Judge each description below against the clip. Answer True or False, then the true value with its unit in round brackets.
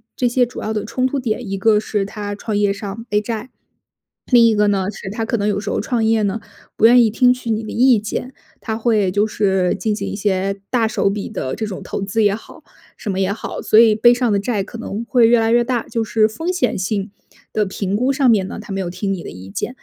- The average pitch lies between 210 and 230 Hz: True (215 Hz)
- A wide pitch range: False (2.6 semitones)